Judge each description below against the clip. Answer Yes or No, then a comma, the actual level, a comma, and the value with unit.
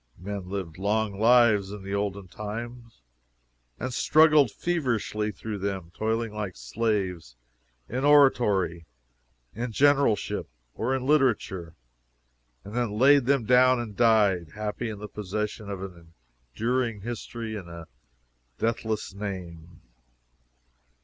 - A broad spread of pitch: No, average, 3.7 semitones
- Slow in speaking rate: Yes, slow, 120 wpm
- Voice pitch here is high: No, low, 105 Hz